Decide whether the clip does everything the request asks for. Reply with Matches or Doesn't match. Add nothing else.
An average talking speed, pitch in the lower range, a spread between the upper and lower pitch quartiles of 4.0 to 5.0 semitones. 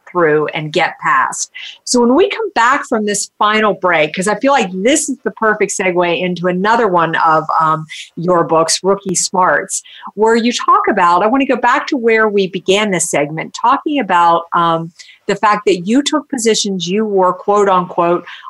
Doesn't match